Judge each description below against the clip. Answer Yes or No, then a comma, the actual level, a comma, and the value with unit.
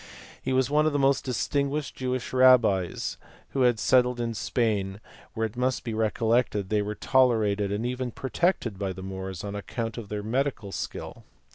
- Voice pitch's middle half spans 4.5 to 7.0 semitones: No, average, 3.9 semitones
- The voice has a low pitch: Yes, low, 115 Hz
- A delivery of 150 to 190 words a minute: Yes, average, 180 wpm